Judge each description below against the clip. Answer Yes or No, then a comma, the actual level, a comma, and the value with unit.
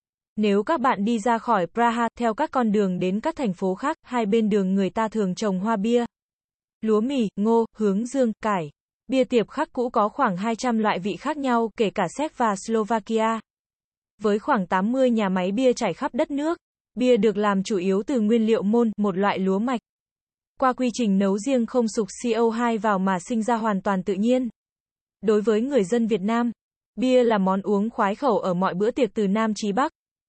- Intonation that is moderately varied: Yes, average, 3.0 semitones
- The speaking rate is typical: Yes, average, 210 wpm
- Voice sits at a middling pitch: No, high, 225 Hz